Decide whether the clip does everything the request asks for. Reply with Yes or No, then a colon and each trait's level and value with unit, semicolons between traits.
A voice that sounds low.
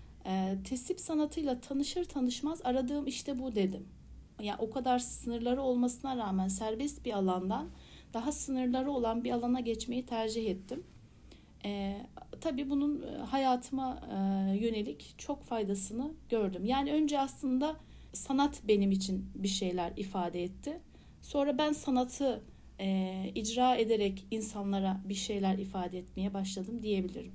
No: high, 235 Hz